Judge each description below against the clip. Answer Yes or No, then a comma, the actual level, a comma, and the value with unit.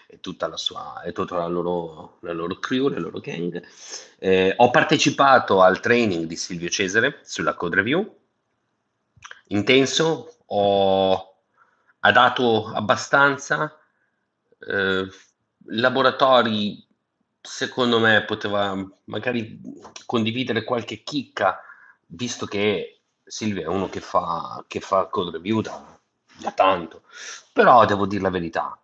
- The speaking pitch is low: Yes, low, 110 Hz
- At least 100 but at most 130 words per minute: Yes, average, 120 wpm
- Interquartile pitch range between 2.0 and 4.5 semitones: No, average, 5.2 semitones